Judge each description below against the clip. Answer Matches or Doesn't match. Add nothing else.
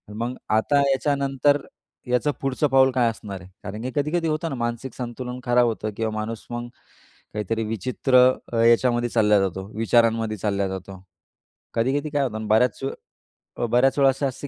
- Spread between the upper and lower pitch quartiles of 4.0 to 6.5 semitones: Doesn't match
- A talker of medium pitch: Doesn't match